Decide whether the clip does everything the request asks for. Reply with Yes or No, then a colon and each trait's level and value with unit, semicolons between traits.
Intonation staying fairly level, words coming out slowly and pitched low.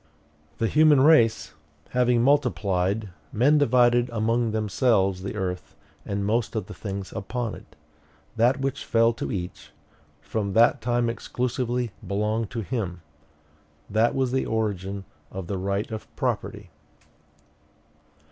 No: average, 3.5 semitones; slow, 130 wpm; low, 115 Hz